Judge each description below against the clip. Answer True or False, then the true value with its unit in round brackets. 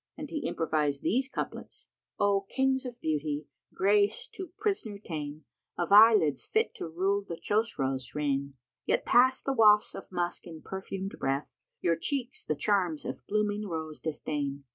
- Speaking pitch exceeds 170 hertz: True (190 Hz)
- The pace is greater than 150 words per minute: True (165 wpm)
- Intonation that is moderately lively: False (6.0 semitones)